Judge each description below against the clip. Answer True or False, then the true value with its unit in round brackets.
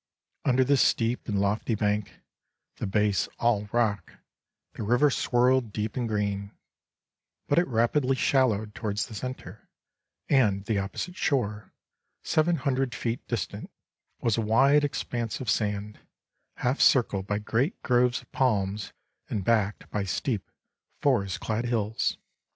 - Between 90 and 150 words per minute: True (135 wpm)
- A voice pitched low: True (115 Hz)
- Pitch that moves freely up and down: False (3.7 semitones)